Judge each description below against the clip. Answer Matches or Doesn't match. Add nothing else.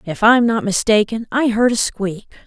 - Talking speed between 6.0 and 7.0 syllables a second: Doesn't match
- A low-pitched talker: Doesn't match